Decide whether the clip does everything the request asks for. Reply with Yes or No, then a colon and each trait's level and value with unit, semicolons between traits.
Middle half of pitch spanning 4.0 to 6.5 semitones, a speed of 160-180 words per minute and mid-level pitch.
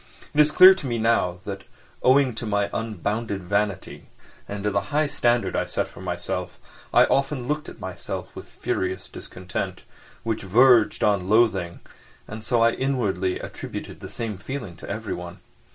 No: average, 4.3 semitones; average, 165 wpm; low, 110 Hz